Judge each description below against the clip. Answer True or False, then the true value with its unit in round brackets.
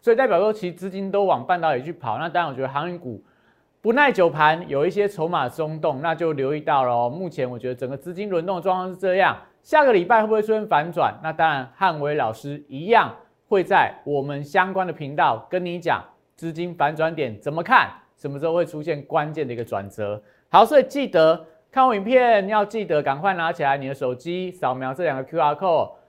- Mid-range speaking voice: True (160 Hz)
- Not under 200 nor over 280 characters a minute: False (335 characters per minute)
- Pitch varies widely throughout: False (4.9 semitones)